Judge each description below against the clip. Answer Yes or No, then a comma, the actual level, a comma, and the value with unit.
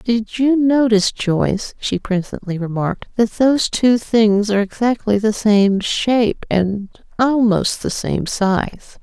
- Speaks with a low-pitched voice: No, high, 215 Hz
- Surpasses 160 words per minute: No, average, 140 wpm